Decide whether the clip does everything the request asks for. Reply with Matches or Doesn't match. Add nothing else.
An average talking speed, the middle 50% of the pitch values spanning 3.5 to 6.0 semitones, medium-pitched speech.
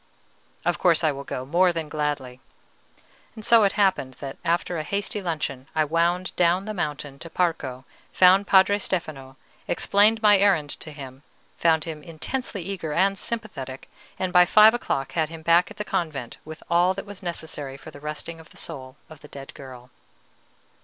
Matches